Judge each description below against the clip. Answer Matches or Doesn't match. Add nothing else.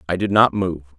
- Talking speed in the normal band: Doesn't match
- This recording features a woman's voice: Doesn't match